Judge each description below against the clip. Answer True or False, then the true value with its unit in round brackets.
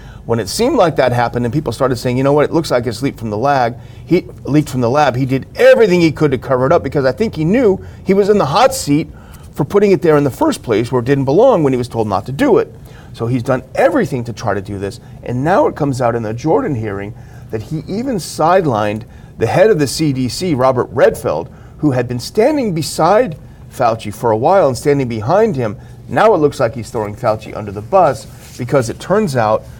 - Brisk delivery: True (245 wpm)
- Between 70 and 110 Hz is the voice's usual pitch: False (135 Hz)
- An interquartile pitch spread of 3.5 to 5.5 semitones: True (4.7 semitones)